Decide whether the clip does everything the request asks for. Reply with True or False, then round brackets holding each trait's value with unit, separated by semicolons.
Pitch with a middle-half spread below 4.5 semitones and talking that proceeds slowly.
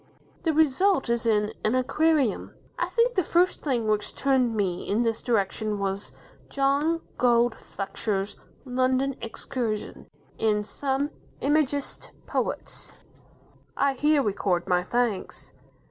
False (4.9 semitones; 120 wpm)